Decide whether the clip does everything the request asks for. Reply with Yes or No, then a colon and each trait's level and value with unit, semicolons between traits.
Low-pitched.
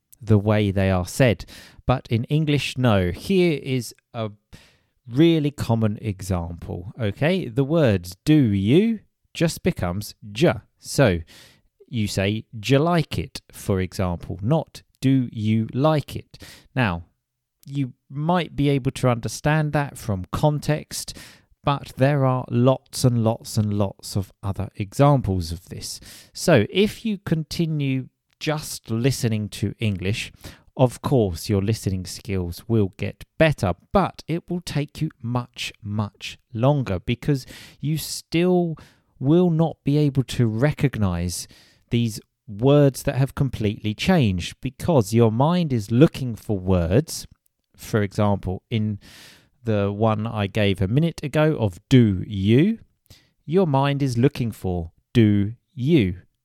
Yes: low, 120 Hz